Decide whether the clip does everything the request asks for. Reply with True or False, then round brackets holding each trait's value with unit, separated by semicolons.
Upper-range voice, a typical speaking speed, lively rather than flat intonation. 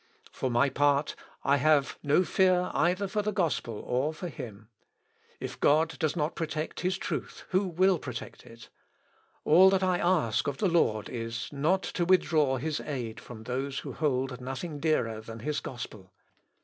False (150 Hz; 170 wpm; 5.9 semitones)